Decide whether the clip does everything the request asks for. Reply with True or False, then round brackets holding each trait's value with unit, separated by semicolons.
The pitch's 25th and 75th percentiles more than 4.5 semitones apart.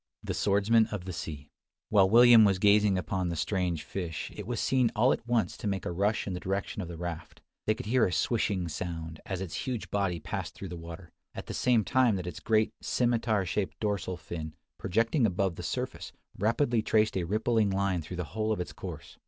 False (3.8 semitones)